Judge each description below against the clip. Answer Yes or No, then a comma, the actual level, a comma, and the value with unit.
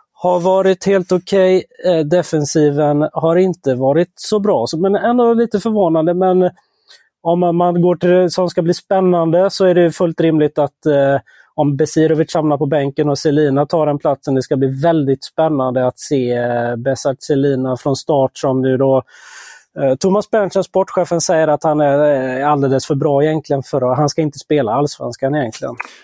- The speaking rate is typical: Yes, average, 175 wpm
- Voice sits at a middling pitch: Yes, medium, 155 Hz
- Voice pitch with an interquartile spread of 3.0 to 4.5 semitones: Yes, average, 4.2 semitones